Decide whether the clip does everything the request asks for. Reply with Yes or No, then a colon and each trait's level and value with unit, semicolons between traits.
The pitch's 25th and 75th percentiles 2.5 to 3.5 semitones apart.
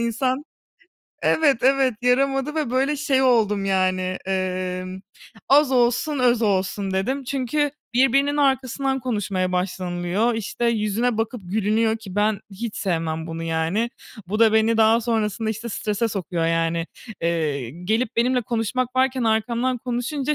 No: average, 5.1 semitones